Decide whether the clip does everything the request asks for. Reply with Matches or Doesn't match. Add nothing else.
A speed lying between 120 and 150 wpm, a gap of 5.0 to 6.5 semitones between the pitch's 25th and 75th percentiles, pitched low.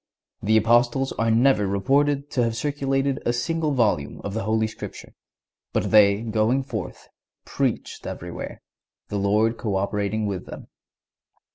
Doesn't match